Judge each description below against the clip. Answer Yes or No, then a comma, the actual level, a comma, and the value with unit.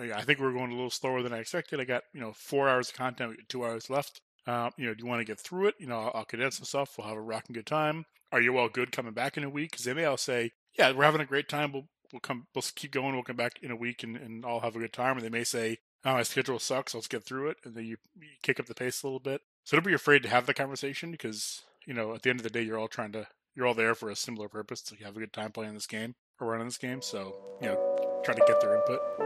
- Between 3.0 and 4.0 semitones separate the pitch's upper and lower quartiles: Yes, average, 3.4 semitones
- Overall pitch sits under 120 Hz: No, low, 125 Hz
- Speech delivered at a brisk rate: Yes, fast, 320 wpm